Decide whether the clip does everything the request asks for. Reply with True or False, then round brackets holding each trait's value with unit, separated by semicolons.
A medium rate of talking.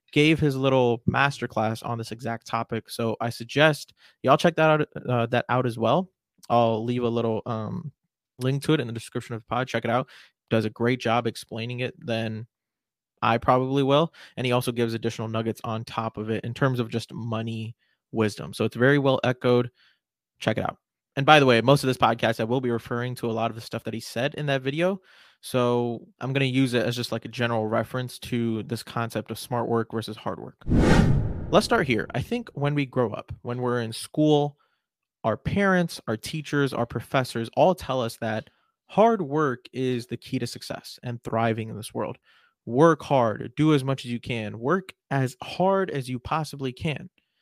False (210 wpm)